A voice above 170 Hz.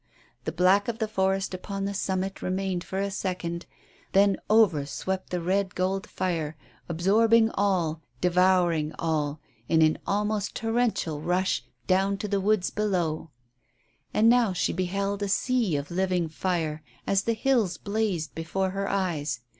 Yes: high, 190 Hz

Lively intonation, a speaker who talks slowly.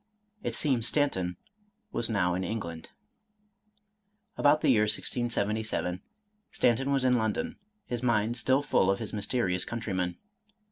No: average, 4.7 semitones; slow, 130 wpm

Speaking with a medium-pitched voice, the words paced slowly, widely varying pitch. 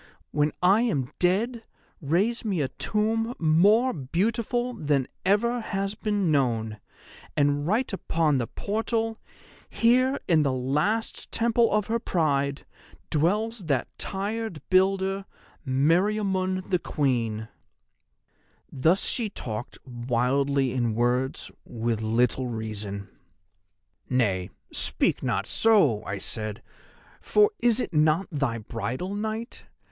Yes: medium, 165 Hz; slow, 115 wpm; wide, 8.8 semitones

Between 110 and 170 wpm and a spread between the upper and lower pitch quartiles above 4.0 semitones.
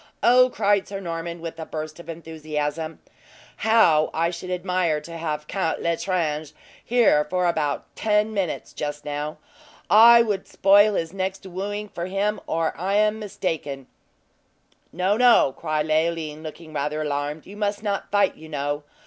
Yes: average, 155 wpm; average, 4.5 semitones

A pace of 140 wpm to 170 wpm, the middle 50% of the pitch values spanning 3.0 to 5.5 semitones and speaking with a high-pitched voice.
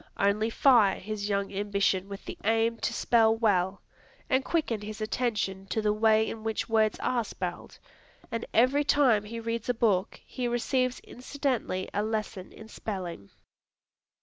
No: average, 155 wpm; narrow, 2.5 semitones; high, 220 Hz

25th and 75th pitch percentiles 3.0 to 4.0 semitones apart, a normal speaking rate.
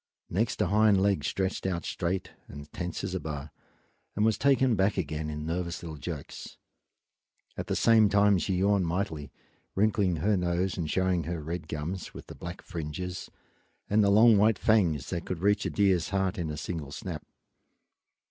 Yes: average, 3.7 semitones; average, 180 wpm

